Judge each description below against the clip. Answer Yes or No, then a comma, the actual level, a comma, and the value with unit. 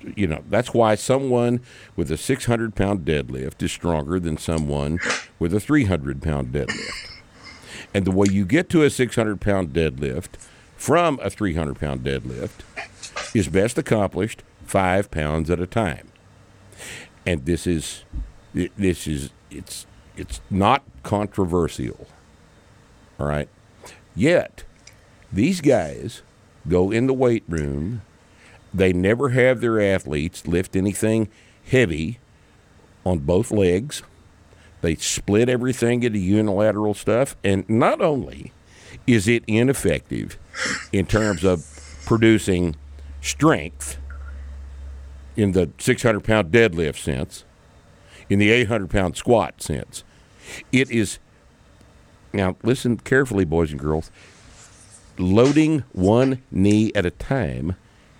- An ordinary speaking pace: No, slow, 115 wpm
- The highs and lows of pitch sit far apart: Yes, wide, 5.7 semitones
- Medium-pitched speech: No, very low, 95 Hz